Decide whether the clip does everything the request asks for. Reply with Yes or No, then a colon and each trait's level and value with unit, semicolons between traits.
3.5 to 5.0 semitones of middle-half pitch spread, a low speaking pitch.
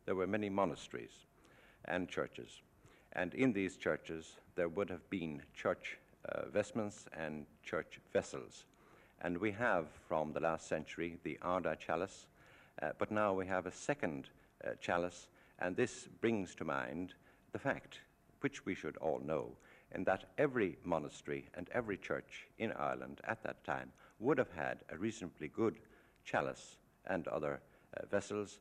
Yes: average, 4.2 semitones; very low, 90 Hz